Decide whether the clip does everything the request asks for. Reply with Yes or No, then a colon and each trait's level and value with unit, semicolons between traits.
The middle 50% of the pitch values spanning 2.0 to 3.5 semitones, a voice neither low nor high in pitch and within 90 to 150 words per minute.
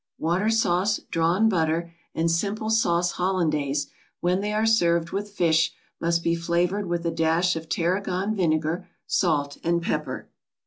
Yes: average, 2.8 semitones; medium, 170 Hz; average, 145 wpm